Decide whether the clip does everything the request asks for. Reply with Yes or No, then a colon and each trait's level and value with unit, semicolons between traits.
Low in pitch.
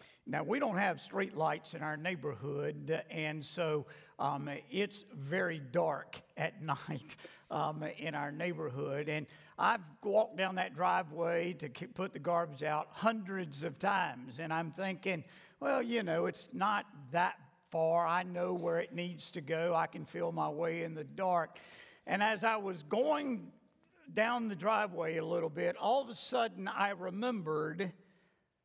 No: medium, 170 Hz